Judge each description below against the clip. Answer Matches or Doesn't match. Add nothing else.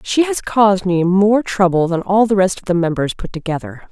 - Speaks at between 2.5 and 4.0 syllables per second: Doesn't match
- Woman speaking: Matches